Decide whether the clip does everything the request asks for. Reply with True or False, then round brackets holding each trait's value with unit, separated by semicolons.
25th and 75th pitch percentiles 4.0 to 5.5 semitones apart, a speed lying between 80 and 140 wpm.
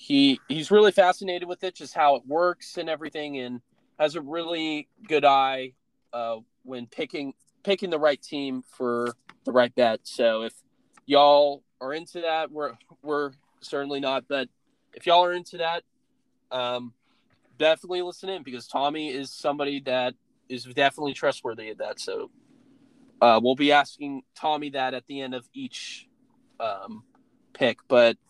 False (5.1 semitones; 155 wpm)